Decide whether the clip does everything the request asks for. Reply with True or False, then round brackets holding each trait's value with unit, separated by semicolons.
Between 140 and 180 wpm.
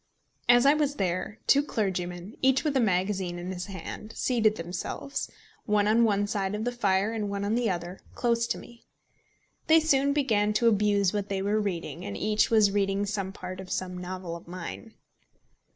False (190 wpm)